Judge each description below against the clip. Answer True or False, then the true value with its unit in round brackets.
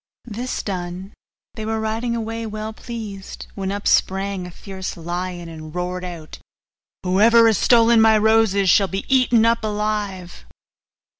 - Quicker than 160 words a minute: False (145 wpm)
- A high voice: True (205 Hz)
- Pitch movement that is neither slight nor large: True (3.4 semitones)